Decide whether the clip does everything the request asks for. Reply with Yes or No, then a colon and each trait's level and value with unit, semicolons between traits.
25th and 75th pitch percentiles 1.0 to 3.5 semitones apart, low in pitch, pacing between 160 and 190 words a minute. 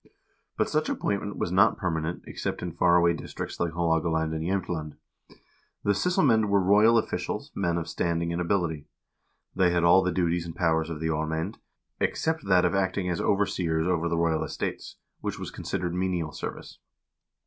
Yes: average, 2.7 semitones; very low, 85 Hz; average, 175 wpm